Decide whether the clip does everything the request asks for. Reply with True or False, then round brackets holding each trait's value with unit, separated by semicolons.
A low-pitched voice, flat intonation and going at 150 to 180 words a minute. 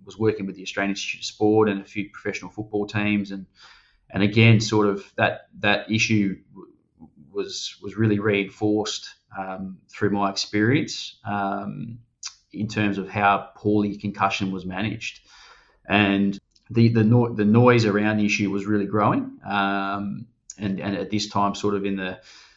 True (105 Hz; 1.5 semitones; 165 wpm)